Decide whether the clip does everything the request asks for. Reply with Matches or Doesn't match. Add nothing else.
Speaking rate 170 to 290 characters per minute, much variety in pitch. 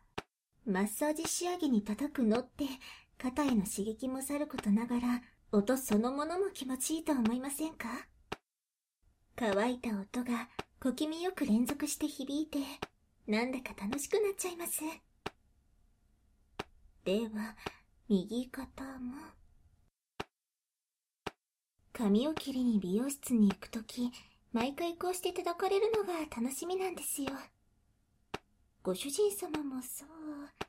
Doesn't match